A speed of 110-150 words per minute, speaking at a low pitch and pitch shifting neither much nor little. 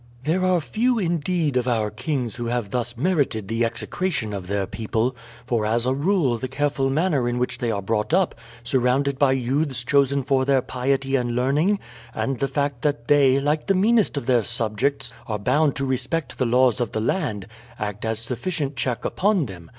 No: average, 195 wpm; low, 130 Hz; average, 3.8 semitones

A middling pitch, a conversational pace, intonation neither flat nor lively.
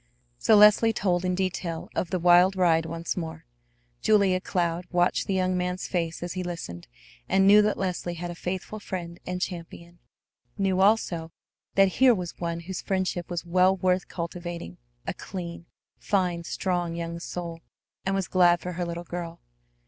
No: medium, 180 Hz; average, 170 wpm; narrow, 1.8 semitones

